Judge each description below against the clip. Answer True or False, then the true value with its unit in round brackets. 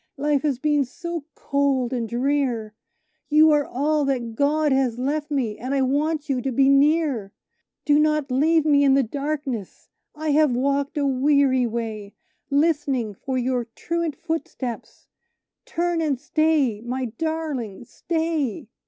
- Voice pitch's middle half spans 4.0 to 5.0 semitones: False (3.3 semitones)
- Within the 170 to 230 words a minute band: False (145 wpm)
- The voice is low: False (280 Hz)